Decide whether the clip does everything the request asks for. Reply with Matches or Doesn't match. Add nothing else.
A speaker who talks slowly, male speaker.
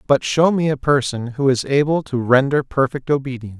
Doesn't match